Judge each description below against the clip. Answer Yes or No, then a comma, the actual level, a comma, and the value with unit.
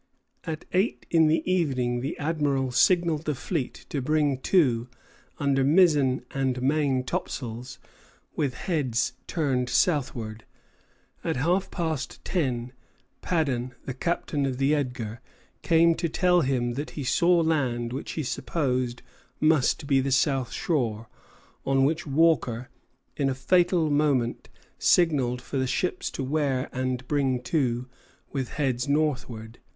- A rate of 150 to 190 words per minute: No, slow, 135 wpm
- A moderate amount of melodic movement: Yes, average, 3.9 semitones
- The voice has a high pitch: No, low, 135 Hz